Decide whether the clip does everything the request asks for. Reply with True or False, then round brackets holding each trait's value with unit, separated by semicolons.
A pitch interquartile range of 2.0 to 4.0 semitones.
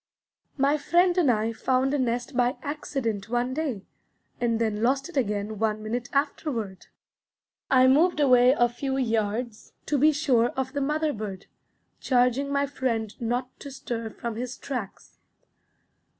True (3.7 semitones)